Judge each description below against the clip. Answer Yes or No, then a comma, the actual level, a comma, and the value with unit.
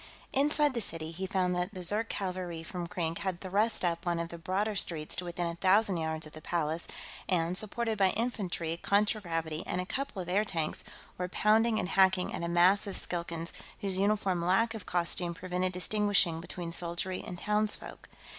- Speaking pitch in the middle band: Yes, medium, 180 Hz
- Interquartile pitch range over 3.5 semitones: No, average, 3.2 semitones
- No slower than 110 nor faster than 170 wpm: No, average, 185 wpm